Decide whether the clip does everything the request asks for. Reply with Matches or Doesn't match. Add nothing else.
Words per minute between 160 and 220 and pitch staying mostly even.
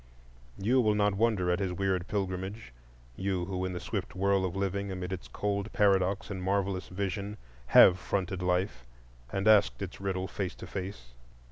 Matches